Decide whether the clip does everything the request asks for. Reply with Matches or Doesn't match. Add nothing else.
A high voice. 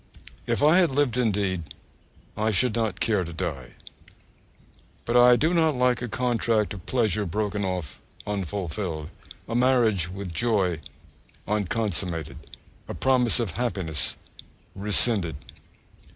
Doesn't match